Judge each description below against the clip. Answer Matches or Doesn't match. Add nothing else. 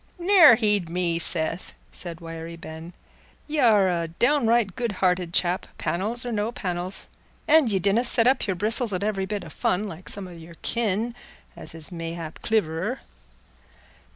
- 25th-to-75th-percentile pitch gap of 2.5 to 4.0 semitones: Doesn't match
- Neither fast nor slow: Matches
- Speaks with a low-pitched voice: Doesn't match